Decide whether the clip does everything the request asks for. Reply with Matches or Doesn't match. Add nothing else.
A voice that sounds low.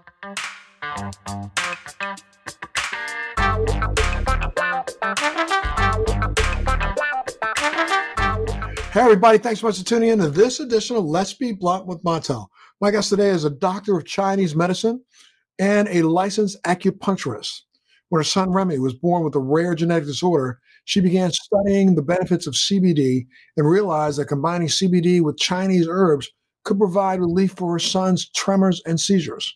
Doesn't match